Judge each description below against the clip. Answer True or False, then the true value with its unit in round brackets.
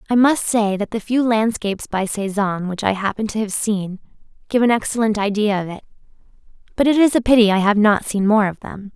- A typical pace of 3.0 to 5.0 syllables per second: False (5.7 syllables/s)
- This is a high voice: True (215 Hz)